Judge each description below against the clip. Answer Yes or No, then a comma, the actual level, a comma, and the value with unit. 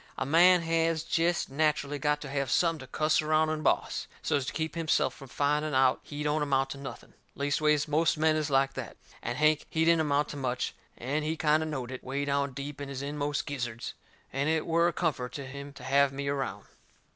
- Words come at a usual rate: No, fast, 220 wpm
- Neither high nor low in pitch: Yes, medium, 145 Hz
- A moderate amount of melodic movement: No, narrow, 2.2 semitones